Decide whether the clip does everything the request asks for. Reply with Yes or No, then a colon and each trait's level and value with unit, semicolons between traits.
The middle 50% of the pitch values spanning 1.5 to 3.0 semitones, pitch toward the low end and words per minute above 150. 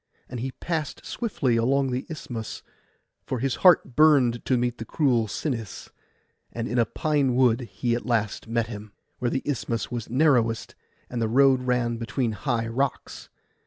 Yes: average, 2.7 semitones; low, 125 Hz; average, 165 wpm